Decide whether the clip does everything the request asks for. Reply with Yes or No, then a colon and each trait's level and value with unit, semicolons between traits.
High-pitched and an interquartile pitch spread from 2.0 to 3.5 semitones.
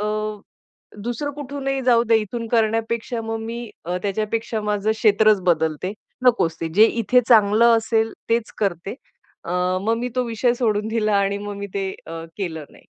Yes: high, 220 Hz; narrow, 2.5 semitones